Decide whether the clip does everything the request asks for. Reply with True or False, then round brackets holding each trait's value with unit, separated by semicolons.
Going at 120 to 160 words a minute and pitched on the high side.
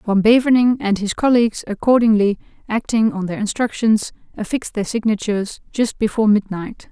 True (140 wpm; 220 Hz)